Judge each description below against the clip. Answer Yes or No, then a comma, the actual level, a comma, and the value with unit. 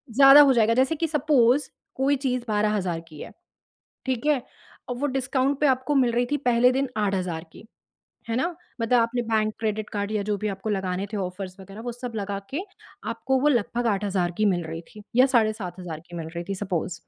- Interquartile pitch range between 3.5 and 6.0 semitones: Yes, average, 5.0 semitones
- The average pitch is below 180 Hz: No, high, 220 Hz